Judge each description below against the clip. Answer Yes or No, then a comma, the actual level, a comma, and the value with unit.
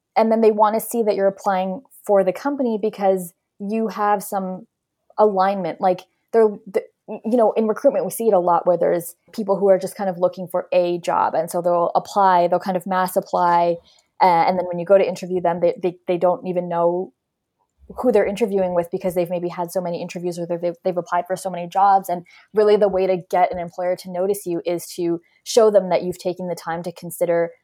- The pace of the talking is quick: Yes, fast, 230 wpm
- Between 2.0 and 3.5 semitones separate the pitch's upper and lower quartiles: Yes, average, 2.8 semitones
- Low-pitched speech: No, medium, 185 Hz